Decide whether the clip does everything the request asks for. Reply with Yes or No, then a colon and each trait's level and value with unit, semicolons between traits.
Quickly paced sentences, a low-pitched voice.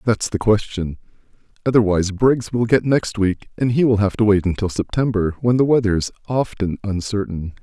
No: average, 175 wpm; low, 105 Hz